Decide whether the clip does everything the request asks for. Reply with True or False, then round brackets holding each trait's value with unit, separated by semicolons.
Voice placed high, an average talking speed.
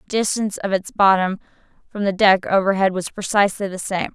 True (195 Hz; 190 wpm)